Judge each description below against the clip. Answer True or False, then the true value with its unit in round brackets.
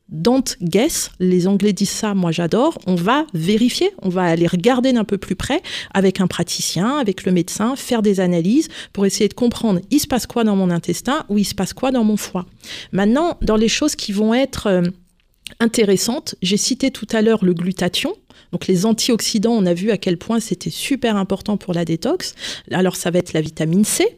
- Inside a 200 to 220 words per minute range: True (210 wpm)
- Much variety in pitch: False (4.4 semitones)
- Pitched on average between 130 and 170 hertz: False (205 Hz)